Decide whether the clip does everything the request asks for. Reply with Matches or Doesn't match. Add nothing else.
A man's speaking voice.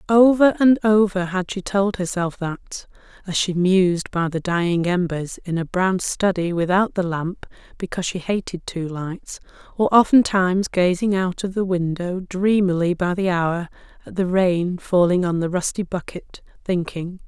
Doesn't match